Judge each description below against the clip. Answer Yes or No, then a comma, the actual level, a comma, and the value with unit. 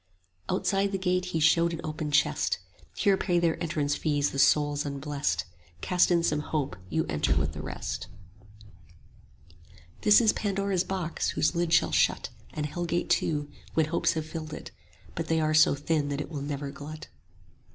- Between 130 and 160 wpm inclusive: No, average, 180 wpm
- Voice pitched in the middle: Yes, medium, 155 Hz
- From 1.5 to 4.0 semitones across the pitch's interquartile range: Yes, average, 3.0 semitones